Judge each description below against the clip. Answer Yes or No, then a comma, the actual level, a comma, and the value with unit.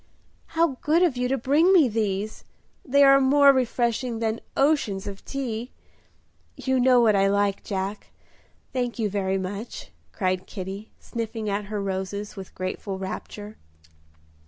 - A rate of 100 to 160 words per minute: Yes, average, 145 wpm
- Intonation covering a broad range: No, average, 4.8 semitones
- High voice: Yes, high, 220 Hz